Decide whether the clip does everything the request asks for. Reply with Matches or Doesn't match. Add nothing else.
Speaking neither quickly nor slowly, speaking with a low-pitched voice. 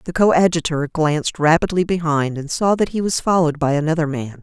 Doesn't match